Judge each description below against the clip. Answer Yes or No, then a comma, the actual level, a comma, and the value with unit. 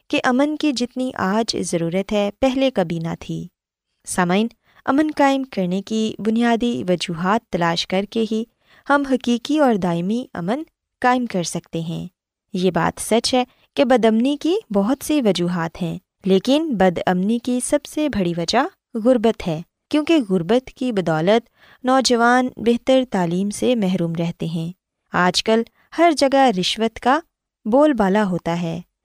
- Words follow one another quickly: No, average, 155 wpm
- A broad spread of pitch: Yes, wide, 6.1 semitones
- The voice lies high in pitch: Yes, high, 225 Hz